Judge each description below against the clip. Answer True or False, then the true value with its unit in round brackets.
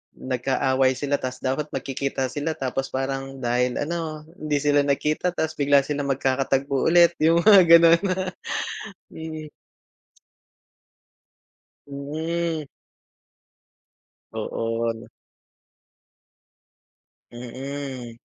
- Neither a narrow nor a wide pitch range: True (3.0 semitones)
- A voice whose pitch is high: False (140 Hz)